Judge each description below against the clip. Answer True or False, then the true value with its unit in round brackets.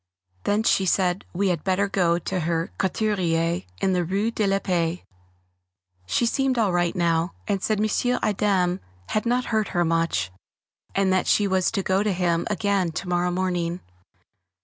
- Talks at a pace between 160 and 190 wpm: True (170 wpm)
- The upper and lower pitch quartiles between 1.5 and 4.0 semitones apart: True (2.7 semitones)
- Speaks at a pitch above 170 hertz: True (185 Hz)